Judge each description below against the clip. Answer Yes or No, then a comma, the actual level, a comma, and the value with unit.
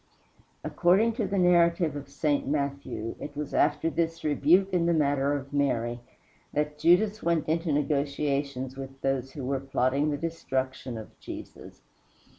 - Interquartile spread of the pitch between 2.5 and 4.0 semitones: Yes, average, 3.5 semitones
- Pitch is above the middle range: No, medium, 145 Hz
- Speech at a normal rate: Yes, average, 150 wpm